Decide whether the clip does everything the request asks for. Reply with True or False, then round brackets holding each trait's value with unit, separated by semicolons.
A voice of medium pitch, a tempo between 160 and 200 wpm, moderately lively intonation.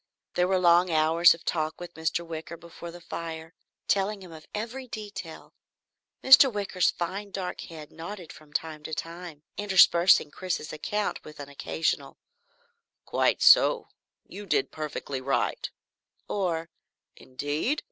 False (170 Hz; 135 wpm; 3.3 semitones)